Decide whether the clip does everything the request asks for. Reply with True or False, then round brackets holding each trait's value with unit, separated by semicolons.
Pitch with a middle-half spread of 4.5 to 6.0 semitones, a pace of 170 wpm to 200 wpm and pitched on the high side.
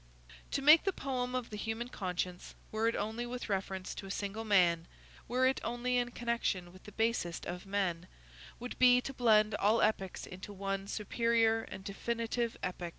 False (3.7 semitones; 180 wpm; 220 Hz)